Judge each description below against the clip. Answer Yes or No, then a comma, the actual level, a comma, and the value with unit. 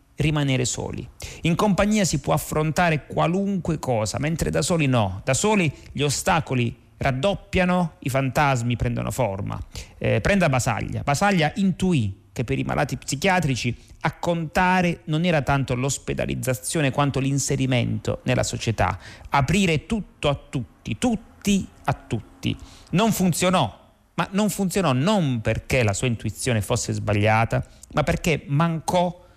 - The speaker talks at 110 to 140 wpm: Yes, average, 130 wpm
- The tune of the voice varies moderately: No, wide, 6.4 semitones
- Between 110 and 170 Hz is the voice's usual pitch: Yes, medium, 140 Hz